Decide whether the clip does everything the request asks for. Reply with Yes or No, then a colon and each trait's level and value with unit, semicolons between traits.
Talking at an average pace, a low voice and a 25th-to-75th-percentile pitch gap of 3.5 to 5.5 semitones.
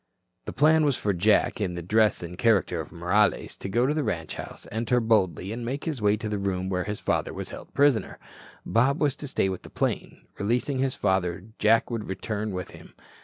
No: fast, 220 wpm; low, 105 Hz; average, 4.5 semitones